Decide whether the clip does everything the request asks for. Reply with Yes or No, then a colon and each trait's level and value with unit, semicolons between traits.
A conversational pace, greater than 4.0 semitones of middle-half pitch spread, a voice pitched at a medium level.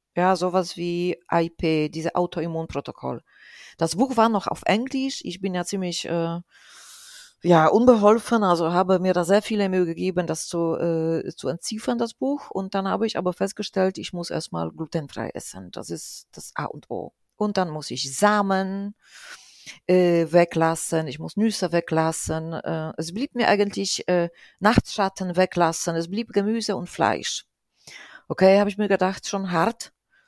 No: average, 160 wpm; average, 3.7 semitones; medium, 180 Hz